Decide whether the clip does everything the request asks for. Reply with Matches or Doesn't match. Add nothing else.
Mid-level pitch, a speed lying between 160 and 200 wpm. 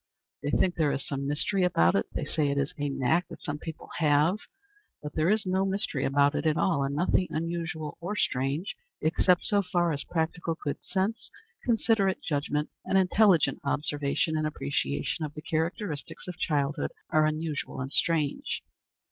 Matches